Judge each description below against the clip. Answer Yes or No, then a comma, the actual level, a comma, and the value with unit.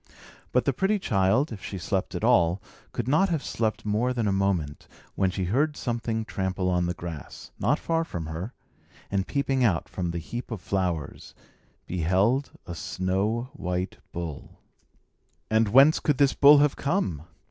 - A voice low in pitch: Yes, low, 100 Hz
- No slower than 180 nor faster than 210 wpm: No, average, 170 wpm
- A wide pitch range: Yes, wide, 6.6 semitones